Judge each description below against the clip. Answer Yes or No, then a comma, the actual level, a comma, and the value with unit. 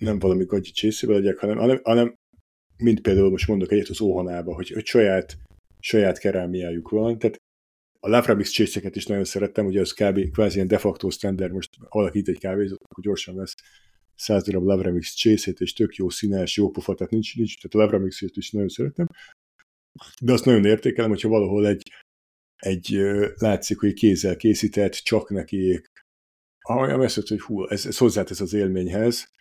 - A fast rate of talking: Yes, fast, 175 wpm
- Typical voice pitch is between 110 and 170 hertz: No, low, 100 Hz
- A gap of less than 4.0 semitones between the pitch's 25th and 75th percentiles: Yes, narrow, 2.4 semitones